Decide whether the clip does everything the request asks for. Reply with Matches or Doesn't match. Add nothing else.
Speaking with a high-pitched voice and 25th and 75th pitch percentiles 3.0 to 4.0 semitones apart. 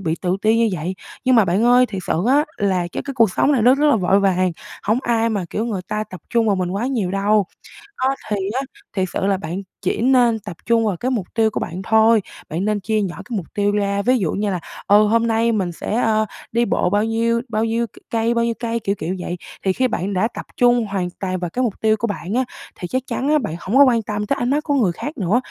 Matches